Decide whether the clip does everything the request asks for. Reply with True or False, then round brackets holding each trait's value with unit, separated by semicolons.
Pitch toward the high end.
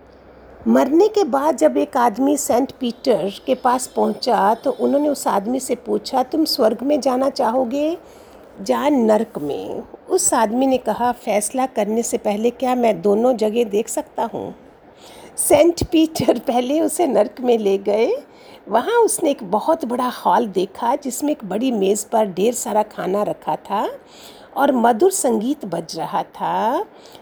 True (250 Hz)